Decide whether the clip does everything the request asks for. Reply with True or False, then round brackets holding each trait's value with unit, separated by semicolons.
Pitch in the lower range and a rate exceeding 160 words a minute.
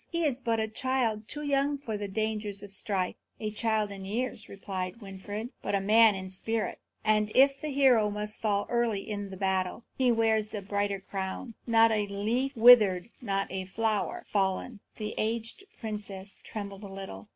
False (215 Hz; 180 wpm)